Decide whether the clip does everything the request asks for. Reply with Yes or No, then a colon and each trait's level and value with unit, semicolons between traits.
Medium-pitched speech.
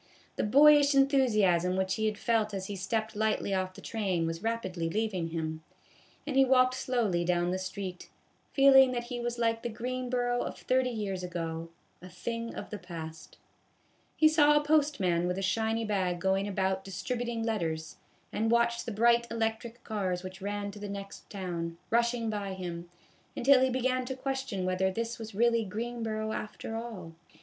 No: high, 215 Hz